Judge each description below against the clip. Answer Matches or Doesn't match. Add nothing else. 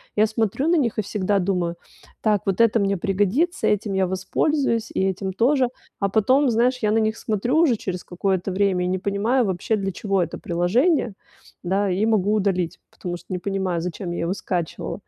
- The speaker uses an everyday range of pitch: Matches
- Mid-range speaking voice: Doesn't match